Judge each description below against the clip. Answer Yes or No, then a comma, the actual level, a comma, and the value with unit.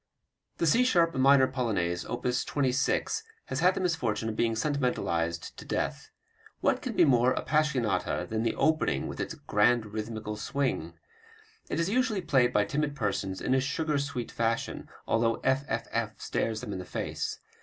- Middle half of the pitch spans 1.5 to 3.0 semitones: No, average, 4.7 semitones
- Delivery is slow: No, average, 165 wpm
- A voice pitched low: Yes, low, 125 Hz